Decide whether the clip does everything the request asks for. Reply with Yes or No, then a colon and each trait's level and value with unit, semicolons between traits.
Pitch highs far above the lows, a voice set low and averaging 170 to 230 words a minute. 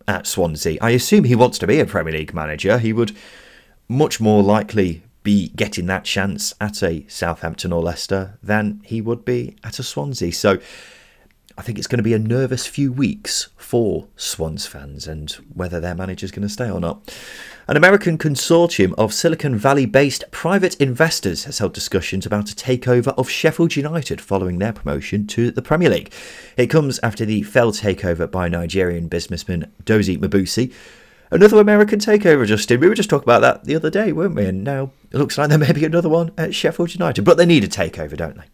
Yes: wide, 6.6 semitones; low, 110 Hz; average, 200 wpm